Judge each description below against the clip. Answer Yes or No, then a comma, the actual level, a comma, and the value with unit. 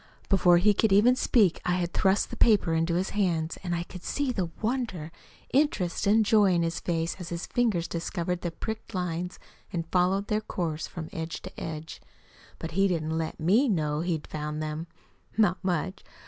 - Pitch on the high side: No, medium, 180 Hz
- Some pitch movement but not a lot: Yes, average, 3.5 semitones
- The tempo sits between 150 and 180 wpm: No, average, 190 wpm